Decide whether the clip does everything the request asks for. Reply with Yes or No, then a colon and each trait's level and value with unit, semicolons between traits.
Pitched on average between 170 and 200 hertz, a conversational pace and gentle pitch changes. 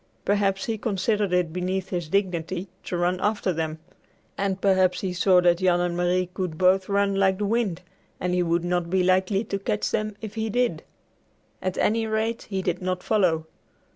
Yes: medium, 185 Hz; average, 190 wpm; narrow, 2.1 semitones